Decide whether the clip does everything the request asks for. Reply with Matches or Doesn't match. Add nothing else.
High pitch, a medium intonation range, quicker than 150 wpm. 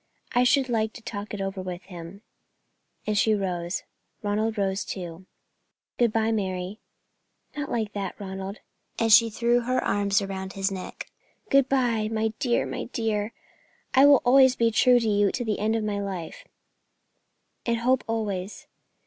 Matches